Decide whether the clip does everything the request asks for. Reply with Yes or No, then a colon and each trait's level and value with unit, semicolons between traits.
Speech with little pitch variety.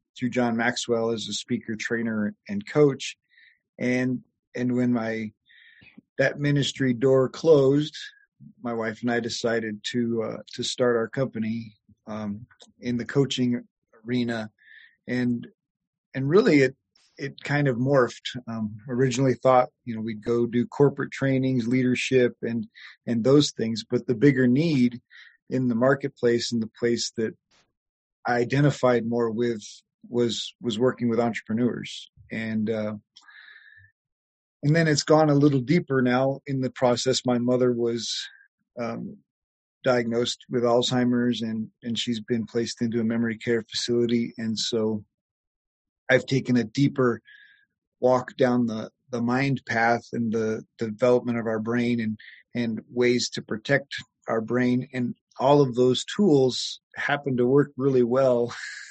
Yes: narrow, 2.3 semitones